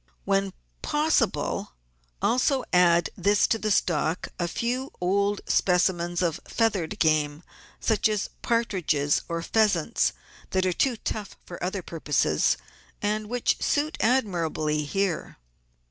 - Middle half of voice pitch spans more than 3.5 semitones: Yes, average, 4.6 semitones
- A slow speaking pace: Yes, slow, 115 wpm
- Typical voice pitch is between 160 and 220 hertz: Yes, high, 190 Hz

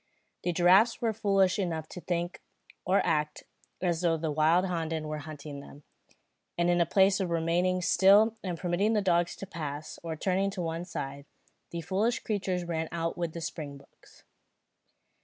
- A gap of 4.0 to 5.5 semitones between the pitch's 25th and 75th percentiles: No, average, 2.9 semitones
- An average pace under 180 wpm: Yes, average, 165 wpm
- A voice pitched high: No, medium, 175 Hz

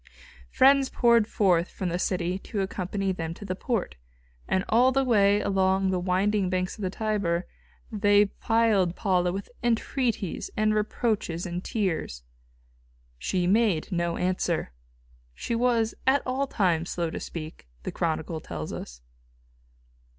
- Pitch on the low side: No, high, 190 Hz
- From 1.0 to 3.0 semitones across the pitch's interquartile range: No, average, 3.9 semitones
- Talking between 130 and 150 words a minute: Yes, average, 145 wpm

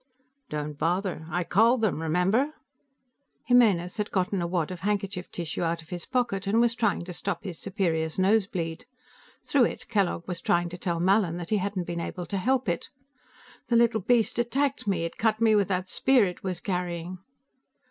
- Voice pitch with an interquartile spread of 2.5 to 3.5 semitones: No, average, 4.2 semitones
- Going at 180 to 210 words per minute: Yes, average, 190 wpm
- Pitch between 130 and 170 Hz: No, high, 190 Hz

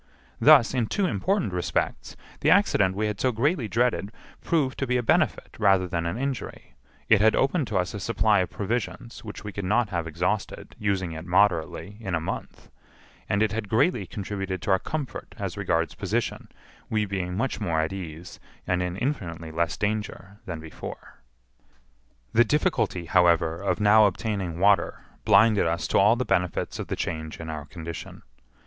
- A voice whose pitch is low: Yes, low, 100 Hz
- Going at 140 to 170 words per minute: No, average, 180 wpm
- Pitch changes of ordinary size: Yes, average, 4.3 semitones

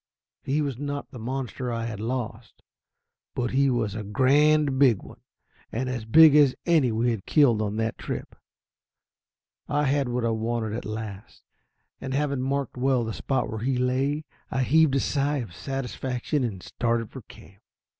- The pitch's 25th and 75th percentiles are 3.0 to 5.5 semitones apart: Yes, average, 3.6 semitones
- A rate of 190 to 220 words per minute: No, average, 170 wpm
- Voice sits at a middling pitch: No, low, 125 Hz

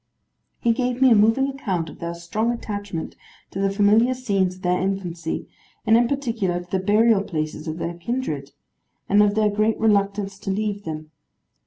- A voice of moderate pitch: No, high, 205 Hz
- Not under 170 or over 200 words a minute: Yes, average, 180 wpm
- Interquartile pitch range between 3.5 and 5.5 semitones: Yes, average, 4.1 semitones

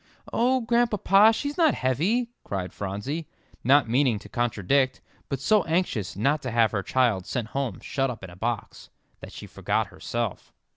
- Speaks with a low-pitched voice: Yes, low, 130 Hz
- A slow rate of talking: No, average, 165 wpm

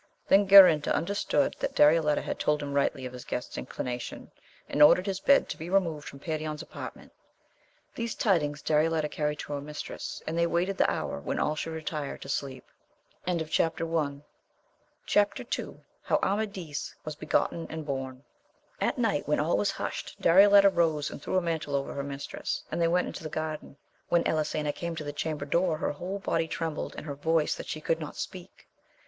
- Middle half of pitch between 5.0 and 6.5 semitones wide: No, average, 2.7 semitones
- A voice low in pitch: No, medium, 155 Hz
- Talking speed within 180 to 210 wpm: Yes, average, 185 wpm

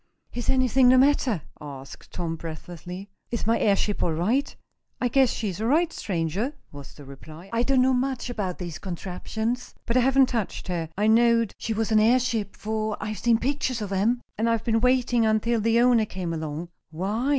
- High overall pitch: Yes, high, 220 Hz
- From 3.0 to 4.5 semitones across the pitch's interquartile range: No, average, 5.2 semitones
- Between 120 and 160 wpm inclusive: No, average, 190 wpm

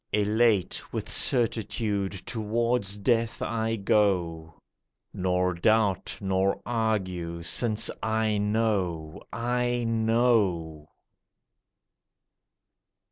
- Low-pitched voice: Yes, low, 105 Hz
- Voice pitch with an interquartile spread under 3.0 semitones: No, average, 3.7 semitones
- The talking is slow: Yes, slow, 75 wpm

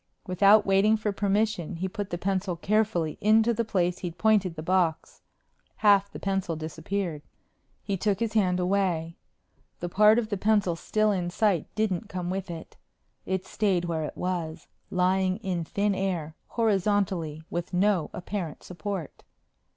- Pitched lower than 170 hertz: No, high, 190 Hz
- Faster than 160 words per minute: No, average, 155 wpm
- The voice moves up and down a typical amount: Yes, average, 3.0 semitones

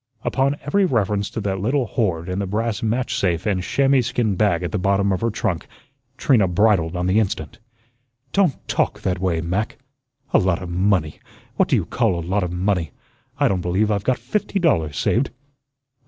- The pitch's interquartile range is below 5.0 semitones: Yes, average, 4.2 semitones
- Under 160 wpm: No, average, 195 wpm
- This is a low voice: Yes, low, 100 Hz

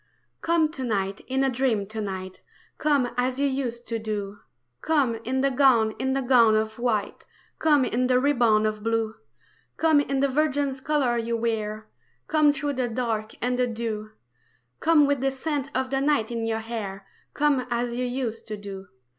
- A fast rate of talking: No, average, 185 wpm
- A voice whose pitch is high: Yes, high, 245 Hz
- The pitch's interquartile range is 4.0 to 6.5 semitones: No, average, 3.6 semitones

